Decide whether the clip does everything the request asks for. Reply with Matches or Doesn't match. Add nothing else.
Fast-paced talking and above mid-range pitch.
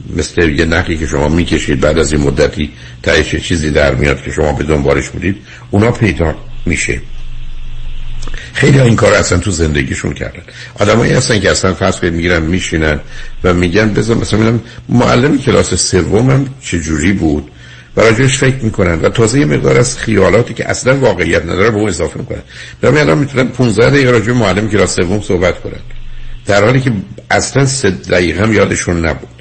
Doesn't match